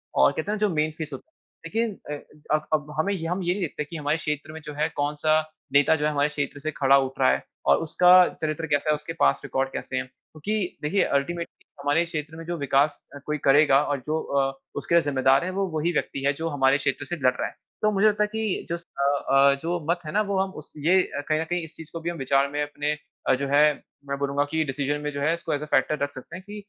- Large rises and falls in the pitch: No, average, 3.1 semitones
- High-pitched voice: No, medium, 150 Hz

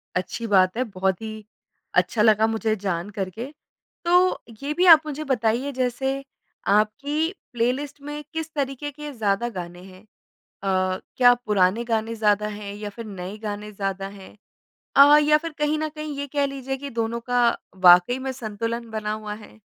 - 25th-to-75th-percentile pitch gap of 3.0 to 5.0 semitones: No, wide, 5.4 semitones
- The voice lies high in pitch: Yes, high, 225 Hz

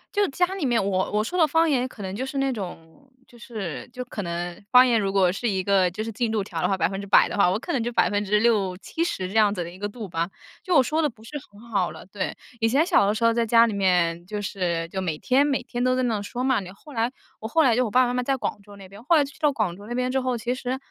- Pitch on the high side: Yes, high, 225 Hz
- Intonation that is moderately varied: Yes, average, 4.7 semitones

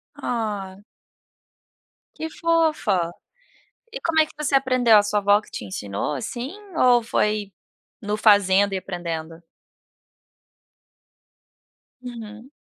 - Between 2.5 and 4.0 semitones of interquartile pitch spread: No, average, 4.9 semitones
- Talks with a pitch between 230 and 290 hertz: No, high, 210 Hz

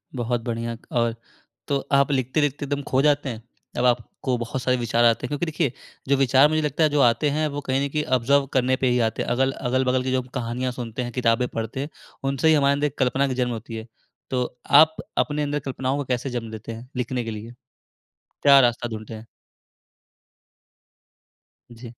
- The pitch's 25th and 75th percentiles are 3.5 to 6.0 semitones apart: No, average, 2.9 semitones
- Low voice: Yes, low, 130 Hz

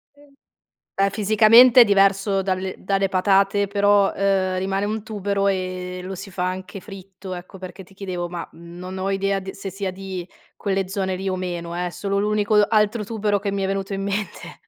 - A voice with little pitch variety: Yes, narrow, 1.4 semitones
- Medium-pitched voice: No, high, 195 Hz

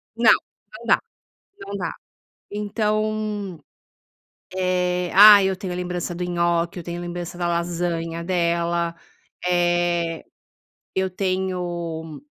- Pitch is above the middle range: No, medium, 175 Hz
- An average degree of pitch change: No, narrow, 1.8 semitones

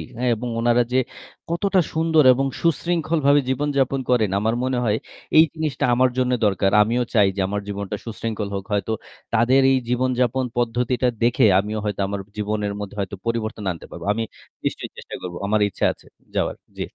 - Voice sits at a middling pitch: No, low, 120 Hz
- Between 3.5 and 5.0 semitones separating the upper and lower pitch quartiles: Yes, average, 4.0 semitones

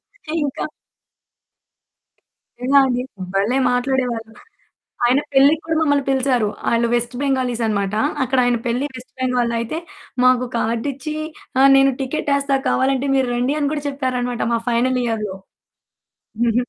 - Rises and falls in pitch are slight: Yes, narrow, 2.3 semitones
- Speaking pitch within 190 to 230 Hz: No, very high, 255 Hz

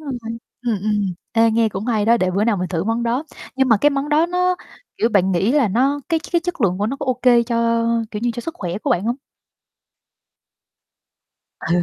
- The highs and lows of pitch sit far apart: No, average, 4.9 semitones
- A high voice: Yes, high, 230 Hz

